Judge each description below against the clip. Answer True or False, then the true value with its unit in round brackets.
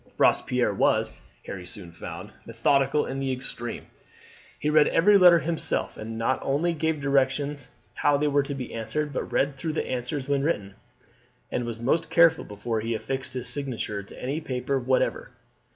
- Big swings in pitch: False (3.7 semitones)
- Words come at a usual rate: True (170 wpm)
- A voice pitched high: False (135 Hz)